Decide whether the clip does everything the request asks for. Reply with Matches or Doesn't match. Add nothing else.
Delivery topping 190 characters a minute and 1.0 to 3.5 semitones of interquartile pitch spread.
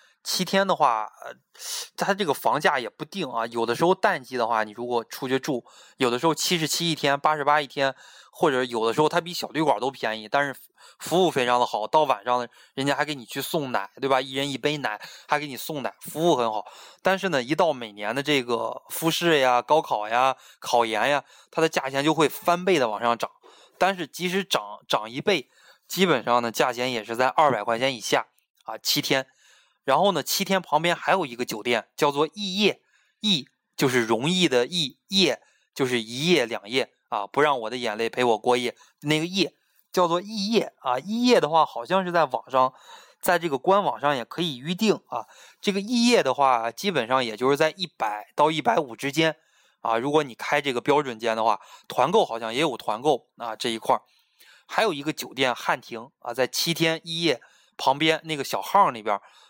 Doesn't match